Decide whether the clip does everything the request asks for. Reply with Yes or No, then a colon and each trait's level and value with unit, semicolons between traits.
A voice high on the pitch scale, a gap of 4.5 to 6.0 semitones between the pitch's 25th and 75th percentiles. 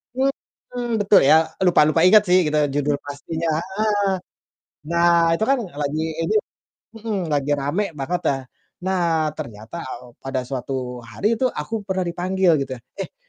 No: medium, 165 Hz; average, 5.2 semitones